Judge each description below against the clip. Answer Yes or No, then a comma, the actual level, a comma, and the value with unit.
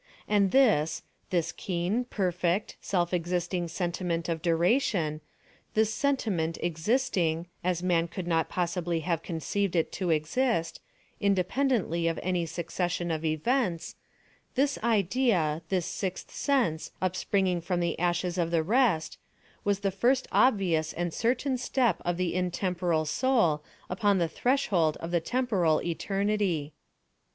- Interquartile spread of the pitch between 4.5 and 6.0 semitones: No, average, 3.6 semitones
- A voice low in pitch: No, medium, 180 Hz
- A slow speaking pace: Yes, slow, 120 wpm